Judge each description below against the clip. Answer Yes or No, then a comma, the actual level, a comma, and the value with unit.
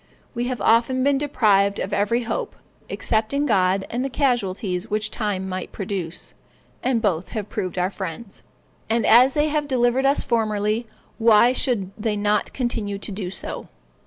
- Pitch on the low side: No, high, 220 Hz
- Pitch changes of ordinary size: Yes, average, 3.9 semitones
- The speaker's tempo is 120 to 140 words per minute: No, average, 165 wpm